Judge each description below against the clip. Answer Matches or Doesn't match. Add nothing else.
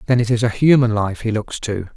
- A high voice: Doesn't match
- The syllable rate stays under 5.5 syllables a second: Doesn't match